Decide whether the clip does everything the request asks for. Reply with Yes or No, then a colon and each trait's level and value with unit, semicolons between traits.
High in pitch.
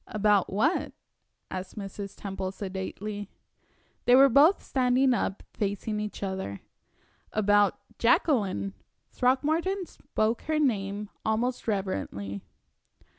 Yes: high, 210 Hz